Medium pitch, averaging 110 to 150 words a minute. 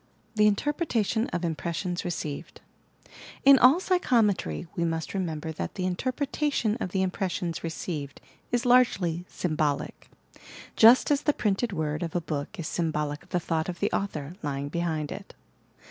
No: medium, 180 Hz; average, 160 wpm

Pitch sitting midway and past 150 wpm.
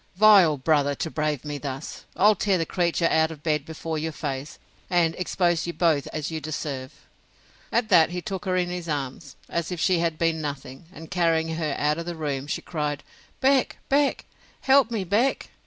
Yes: medium, 160 Hz; average, 200 wpm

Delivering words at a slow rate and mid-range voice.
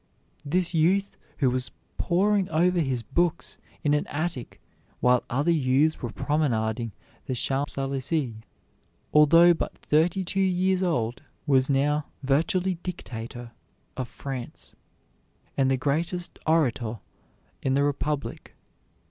Yes: slow, 120 wpm; medium, 145 Hz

